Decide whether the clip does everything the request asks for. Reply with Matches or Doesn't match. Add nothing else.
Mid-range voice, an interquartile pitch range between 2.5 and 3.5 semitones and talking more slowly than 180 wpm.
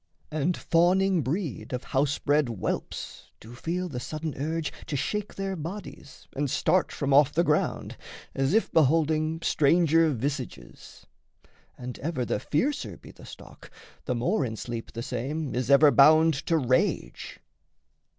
Doesn't match